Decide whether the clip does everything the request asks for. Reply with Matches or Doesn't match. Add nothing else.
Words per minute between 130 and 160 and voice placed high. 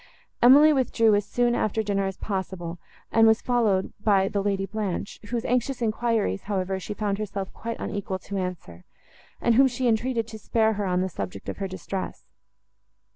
Doesn't match